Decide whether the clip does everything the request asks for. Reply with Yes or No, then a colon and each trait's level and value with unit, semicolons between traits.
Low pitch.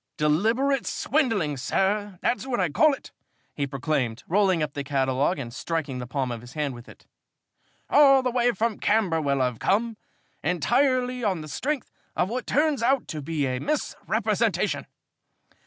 No: medium, 180 Hz